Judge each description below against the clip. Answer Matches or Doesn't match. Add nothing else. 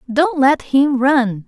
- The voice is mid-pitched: Doesn't match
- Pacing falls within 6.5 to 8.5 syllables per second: Doesn't match